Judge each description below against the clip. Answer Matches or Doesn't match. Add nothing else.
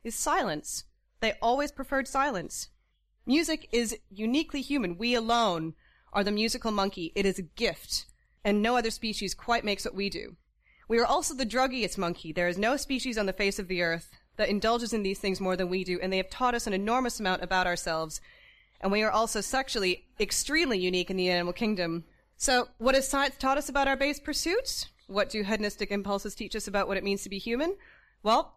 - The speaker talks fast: Matches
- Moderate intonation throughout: Matches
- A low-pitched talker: Doesn't match